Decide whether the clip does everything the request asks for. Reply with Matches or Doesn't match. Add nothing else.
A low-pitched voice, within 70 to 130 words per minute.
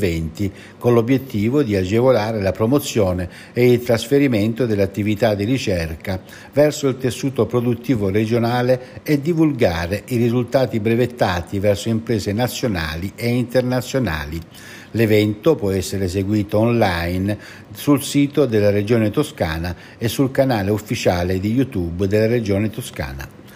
Matches